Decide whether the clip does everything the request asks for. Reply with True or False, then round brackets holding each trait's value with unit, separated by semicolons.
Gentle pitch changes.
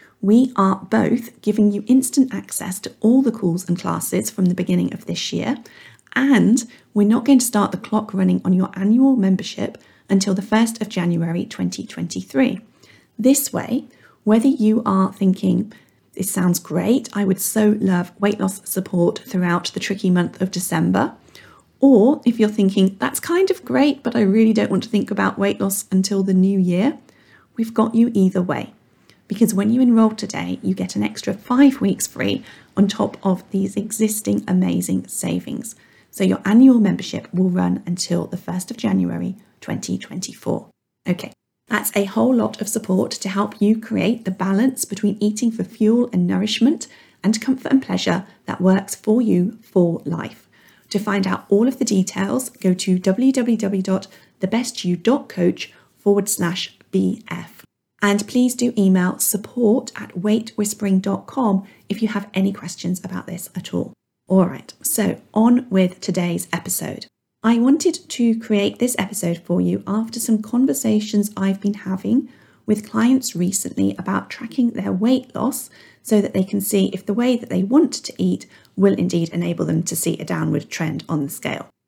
False (3.7 semitones)